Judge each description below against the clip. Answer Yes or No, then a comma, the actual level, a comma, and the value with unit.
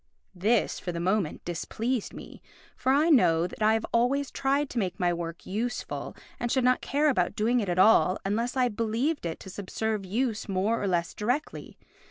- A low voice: No, high, 220 Hz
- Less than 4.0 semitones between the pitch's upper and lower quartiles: No, average, 5.2 semitones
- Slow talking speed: No, average, 195 wpm